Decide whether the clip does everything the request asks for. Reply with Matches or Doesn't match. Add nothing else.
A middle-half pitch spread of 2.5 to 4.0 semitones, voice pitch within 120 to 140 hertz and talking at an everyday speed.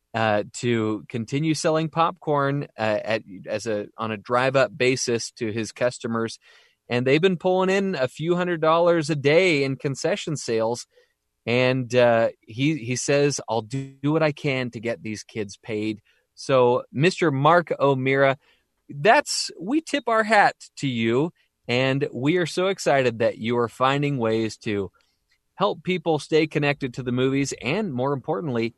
Doesn't match